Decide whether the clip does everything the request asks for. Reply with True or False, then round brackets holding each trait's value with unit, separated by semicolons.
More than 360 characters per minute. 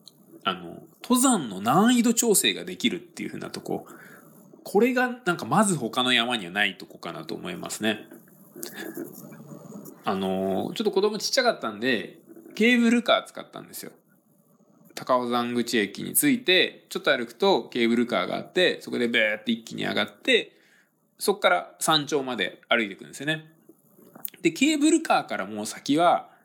False (335 characters per minute)